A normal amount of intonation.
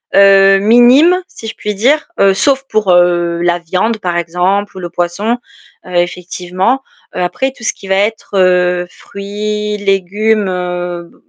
Yes: average, 3.1 semitones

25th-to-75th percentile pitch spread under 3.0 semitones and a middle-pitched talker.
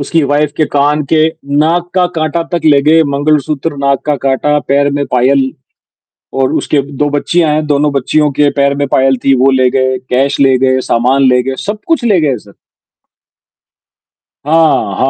Yes: narrow, 2.4 semitones; medium, 145 Hz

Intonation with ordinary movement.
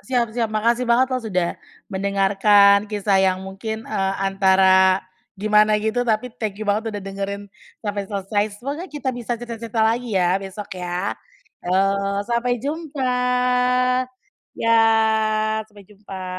Yes: average, 3.2 semitones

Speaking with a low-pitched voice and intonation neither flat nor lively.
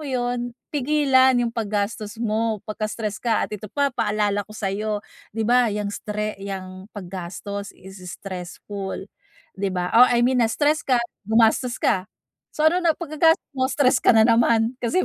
No: high, 220 Hz; average, 3.6 semitones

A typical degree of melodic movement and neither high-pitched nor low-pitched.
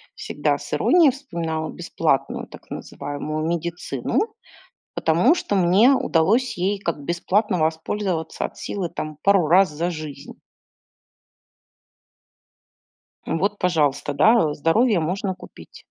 Yes: average, 4.1 semitones; medium, 170 Hz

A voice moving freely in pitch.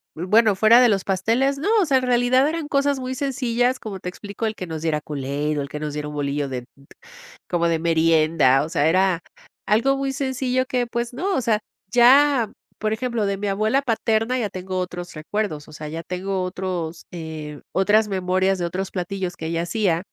Yes: wide, 6.7 semitones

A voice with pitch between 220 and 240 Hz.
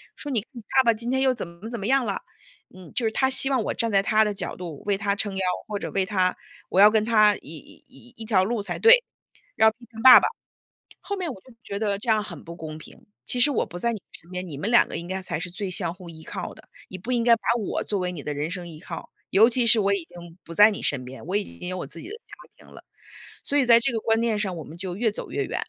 No: high, 205 Hz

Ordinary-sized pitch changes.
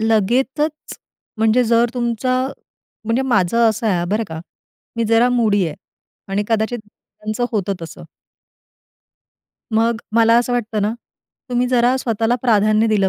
No: narrow, 2.2 semitones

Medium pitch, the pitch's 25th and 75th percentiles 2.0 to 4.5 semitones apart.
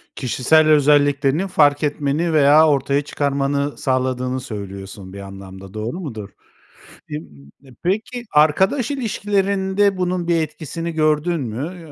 No: medium, 145 Hz; average, 5.0 semitones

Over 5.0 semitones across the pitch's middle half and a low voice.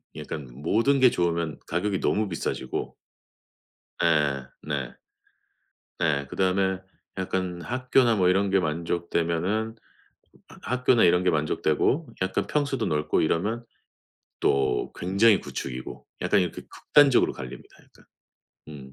Yes: wide, 5.6 semitones; very low, 95 Hz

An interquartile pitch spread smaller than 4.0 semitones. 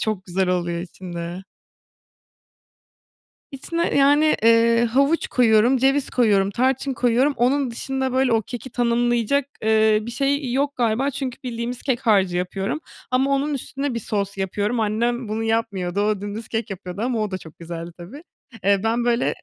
No: average, 4.5 semitones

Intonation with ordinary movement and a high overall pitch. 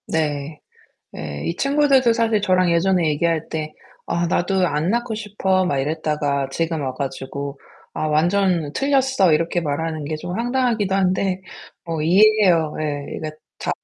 No: average, 4.6 semitones; medium, 170 Hz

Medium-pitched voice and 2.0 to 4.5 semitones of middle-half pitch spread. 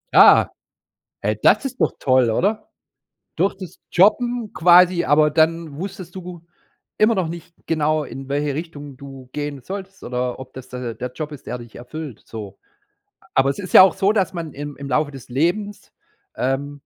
No: medium, 155 Hz; average, 5.3 semitones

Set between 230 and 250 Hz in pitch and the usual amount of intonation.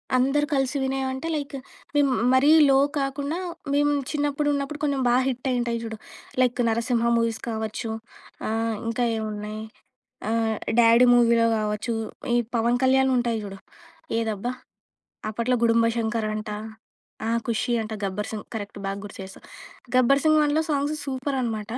Yes: high, 240 Hz; average, 3.4 semitones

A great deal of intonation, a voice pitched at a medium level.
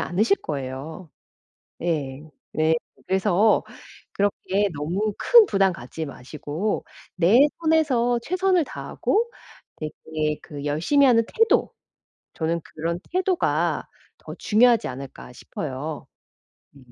Yes: wide, 7.8 semitones; medium, 180 Hz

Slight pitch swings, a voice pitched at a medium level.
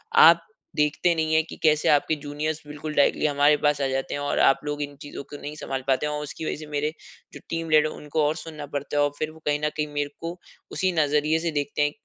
Yes: narrow, 1.3 semitones; medium, 150 Hz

